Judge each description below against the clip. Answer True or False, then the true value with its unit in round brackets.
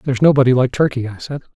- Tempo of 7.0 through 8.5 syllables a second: True (7.5 syllables/s)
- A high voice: False (130 Hz)